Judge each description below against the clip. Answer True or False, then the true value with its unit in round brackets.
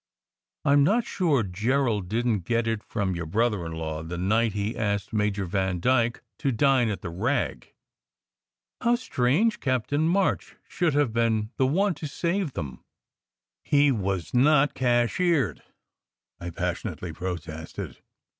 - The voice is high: False (115 Hz)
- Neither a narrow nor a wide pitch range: False (6.8 semitones)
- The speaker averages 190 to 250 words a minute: False (150 wpm)